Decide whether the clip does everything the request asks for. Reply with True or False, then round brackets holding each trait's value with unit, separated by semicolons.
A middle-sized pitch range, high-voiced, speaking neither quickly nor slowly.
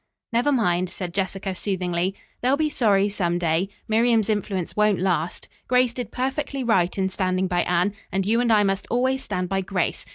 True (4.2 semitones; 195 Hz; 185 wpm)